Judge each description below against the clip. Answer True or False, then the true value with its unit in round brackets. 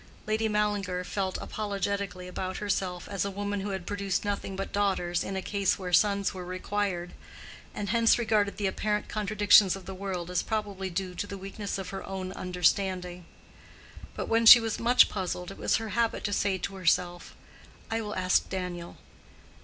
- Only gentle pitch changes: True (2.1 semitones)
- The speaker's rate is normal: True (180 wpm)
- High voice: True (195 Hz)